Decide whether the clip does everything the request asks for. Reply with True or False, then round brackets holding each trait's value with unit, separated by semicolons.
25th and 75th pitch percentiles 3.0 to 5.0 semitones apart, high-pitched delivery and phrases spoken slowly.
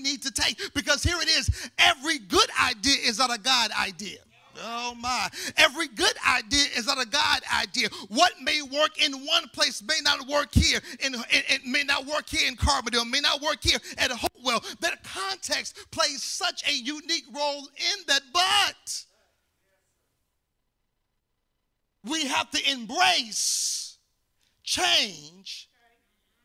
False (3.8 semitones; 285 Hz; 145 wpm)